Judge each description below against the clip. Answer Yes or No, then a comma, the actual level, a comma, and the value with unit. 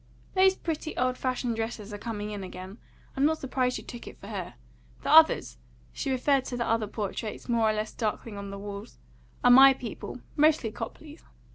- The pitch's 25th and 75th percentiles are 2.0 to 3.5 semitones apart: No, average, 4.2 semitones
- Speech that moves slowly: No, average, 190 wpm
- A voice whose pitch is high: Yes, high, 240 Hz